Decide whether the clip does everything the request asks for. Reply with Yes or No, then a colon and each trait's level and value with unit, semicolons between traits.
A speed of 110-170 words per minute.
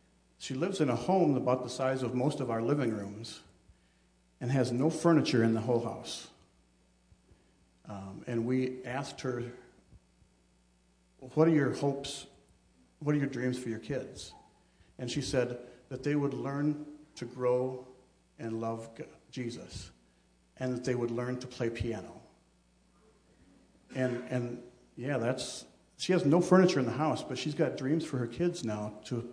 Yes: average, 160 wpm